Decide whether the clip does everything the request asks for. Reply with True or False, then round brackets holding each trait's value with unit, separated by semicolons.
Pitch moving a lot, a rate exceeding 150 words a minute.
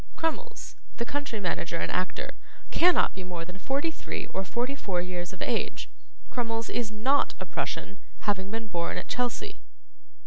True (6.8 semitones; 165 wpm)